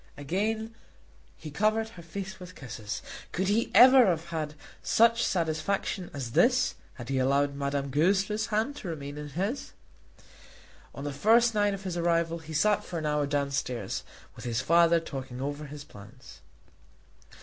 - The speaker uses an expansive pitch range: Yes, wide, 6.3 semitones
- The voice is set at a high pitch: No, medium, 165 Hz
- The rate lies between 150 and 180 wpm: Yes, average, 160 wpm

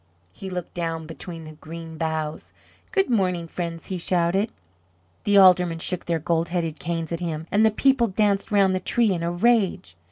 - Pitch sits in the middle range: Yes, medium, 175 Hz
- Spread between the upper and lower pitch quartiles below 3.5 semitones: Yes, average, 3.1 semitones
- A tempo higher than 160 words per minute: Yes, average, 185 wpm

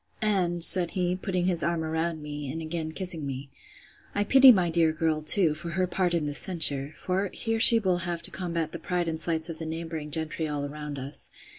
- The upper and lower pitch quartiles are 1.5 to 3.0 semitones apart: Yes, narrow, 2.4 semitones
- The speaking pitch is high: No, medium, 165 Hz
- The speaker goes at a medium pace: No, fast, 220 wpm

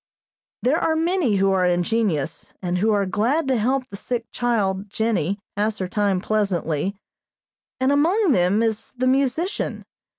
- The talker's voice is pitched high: Yes, high, 215 Hz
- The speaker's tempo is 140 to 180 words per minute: Yes, average, 155 wpm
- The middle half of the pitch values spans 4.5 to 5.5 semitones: Yes, average, 5.2 semitones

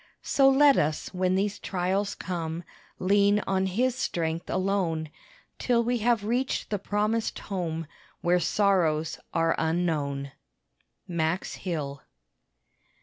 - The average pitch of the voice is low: No, medium, 185 Hz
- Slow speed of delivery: Yes, slow, 115 wpm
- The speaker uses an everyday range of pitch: Yes, average, 4.1 semitones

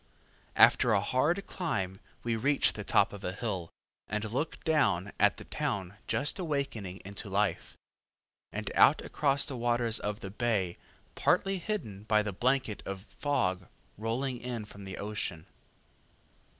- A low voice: Yes, low, 110 Hz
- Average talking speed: Yes, average, 150 wpm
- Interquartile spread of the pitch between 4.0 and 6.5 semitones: Yes, average, 5.3 semitones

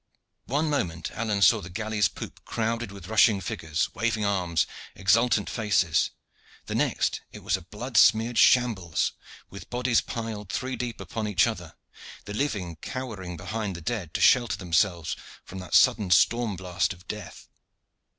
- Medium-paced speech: Yes, average, 155 wpm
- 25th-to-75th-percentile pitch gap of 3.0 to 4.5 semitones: Yes, average, 4.1 semitones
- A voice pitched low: Yes, low, 105 Hz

